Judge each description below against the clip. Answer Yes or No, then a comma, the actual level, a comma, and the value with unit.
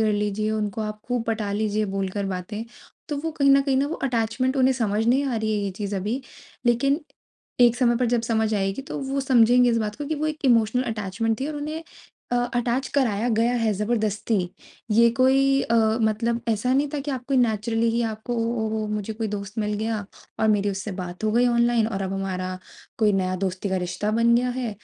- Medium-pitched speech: No, high, 225 Hz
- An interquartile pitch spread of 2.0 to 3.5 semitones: Yes, average, 3.0 semitones